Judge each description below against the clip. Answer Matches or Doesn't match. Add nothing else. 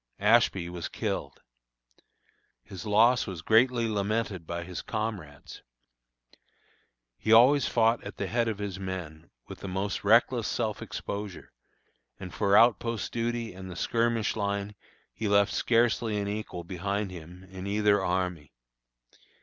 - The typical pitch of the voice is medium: Doesn't match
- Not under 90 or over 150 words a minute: Matches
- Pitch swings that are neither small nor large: Matches